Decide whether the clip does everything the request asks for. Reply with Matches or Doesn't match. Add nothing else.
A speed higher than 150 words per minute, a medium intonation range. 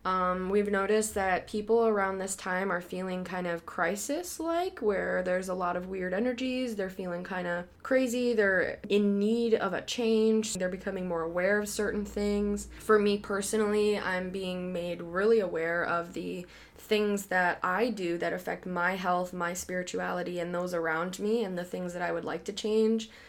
Matches